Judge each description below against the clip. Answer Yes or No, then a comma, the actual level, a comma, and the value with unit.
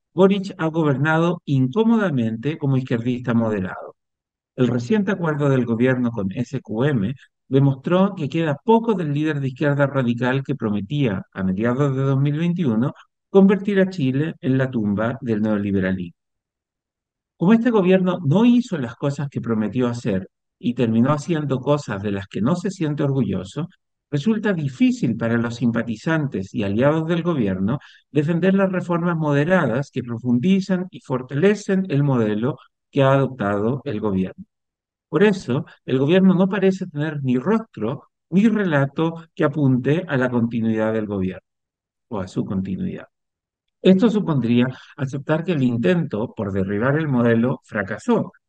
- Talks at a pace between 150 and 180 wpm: No, average, 140 wpm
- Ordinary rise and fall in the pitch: No, wide, 6.6 semitones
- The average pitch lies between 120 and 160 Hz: Yes, low, 135 Hz